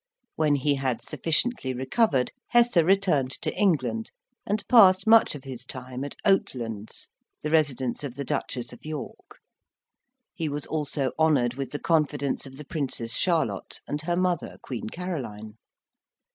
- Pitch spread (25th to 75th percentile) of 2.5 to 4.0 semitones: No, average, 5.0 semitones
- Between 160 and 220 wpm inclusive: No, average, 145 wpm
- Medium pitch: Yes, medium, 145 Hz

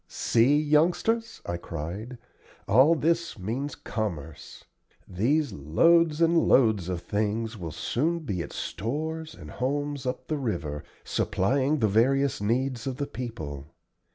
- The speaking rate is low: Yes, slow, 130 wpm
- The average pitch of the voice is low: Yes, low, 125 Hz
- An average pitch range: No, wide, 7.3 semitones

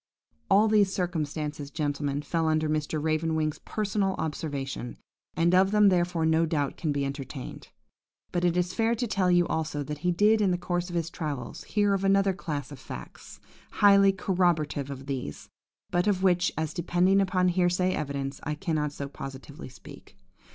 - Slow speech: No, average, 175 wpm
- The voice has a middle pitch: Yes, medium, 165 Hz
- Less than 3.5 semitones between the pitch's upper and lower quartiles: No, average, 4.0 semitones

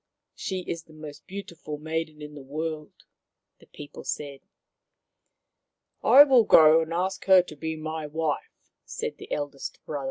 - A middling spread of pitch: No, narrow, 2.0 semitones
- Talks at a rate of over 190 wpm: No, average, 160 wpm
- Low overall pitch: No, medium, 155 Hz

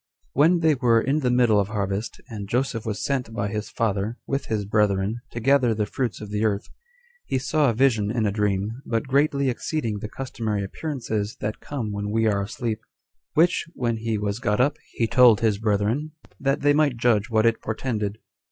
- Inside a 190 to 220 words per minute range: Yes, average, 200 wpm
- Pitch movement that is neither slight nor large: Yes, average, 3.8 semitones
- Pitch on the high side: No, low, 115 Hz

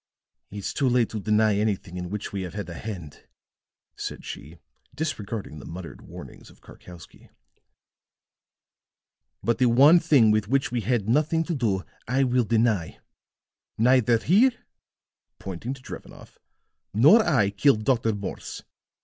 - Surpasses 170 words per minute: No, average, 140 wpm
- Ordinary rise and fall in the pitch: Yes, average, 4.7 semitones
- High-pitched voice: No, low, 110 Hz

